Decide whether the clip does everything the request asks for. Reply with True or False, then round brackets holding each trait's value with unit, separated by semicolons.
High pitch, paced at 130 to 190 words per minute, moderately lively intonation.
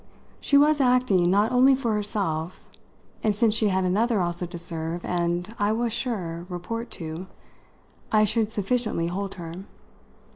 True (205 Hz; 155 wpm; 4.9 semitones)